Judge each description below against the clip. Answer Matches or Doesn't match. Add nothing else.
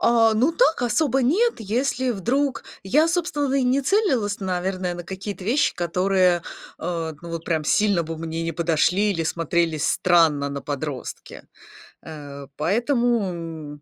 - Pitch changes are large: Matches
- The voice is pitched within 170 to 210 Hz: Matches